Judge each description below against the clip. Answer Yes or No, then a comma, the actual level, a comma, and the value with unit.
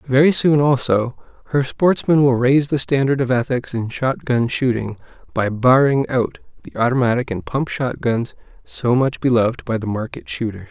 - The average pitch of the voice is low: Yes, low, 125 Hz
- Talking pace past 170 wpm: No, average, 165 wpm